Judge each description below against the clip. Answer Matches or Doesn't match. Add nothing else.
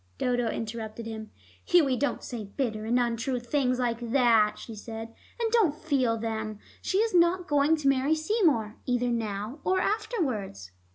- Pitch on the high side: Matches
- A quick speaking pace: Doesn't match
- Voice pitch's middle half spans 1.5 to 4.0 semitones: Doesn't match